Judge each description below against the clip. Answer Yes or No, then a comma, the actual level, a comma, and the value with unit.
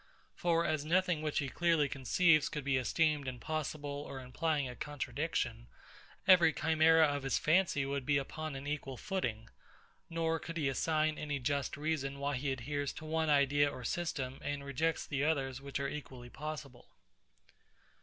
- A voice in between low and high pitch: Yes, medium, 145 Hz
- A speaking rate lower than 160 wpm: No, average, 165 wpm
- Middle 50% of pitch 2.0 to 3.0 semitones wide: Yes, narrow, 2.6 semitones